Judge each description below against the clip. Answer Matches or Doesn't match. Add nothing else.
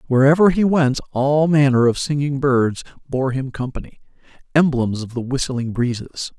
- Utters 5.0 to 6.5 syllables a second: Doesn't match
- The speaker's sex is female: Doesn't match